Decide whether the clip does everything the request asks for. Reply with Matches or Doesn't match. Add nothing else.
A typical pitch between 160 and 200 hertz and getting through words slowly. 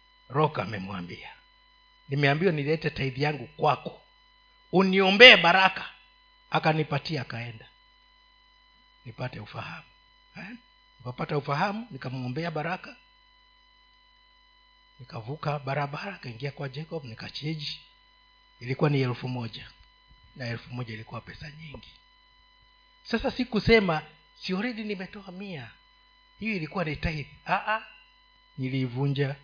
Matches